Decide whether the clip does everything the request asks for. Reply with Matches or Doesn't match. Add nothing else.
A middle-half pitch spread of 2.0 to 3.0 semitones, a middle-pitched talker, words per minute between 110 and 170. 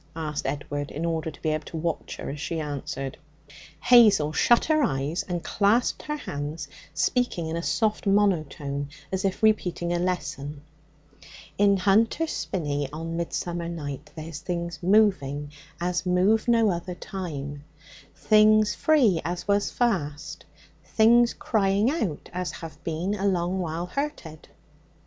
Doesn't match